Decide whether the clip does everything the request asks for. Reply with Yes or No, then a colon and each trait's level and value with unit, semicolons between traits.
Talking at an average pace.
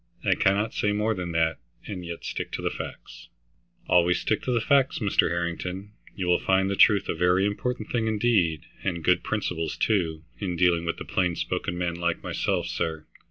Yes: average, 180 wpm